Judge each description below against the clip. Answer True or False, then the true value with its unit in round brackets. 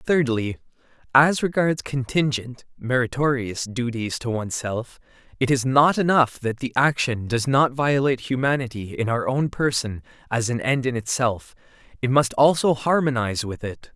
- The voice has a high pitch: False (130 Hz)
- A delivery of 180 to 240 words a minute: False (145 wpm)